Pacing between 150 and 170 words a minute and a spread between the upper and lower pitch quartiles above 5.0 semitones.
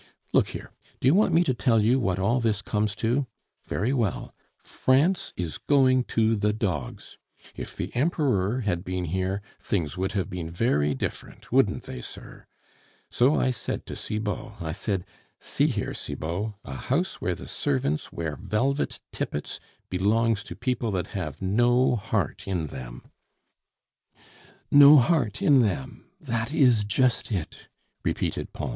Yes: average, 155 wpm; wide, 5.6 semitones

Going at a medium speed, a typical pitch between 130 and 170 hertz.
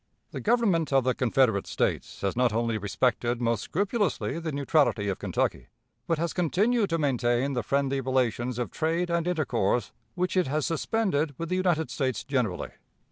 Yes: average, 170 wpm; medium, 140 Hz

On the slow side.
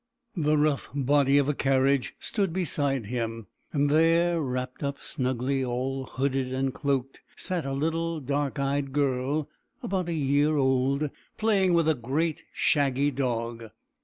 No: average, 145 wpm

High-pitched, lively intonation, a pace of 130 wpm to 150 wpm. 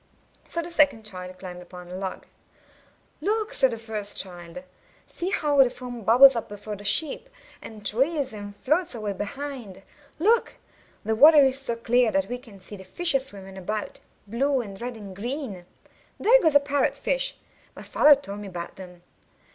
No: high, 230 Hz; wide, 6.2 semitones; average, 180 wpm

